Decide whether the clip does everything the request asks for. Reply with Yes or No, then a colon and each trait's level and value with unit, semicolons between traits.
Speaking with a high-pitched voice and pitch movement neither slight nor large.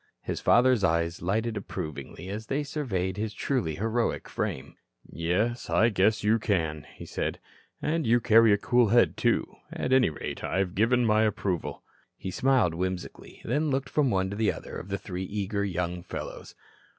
No: low, 105 Hz; average, 4.5 semitones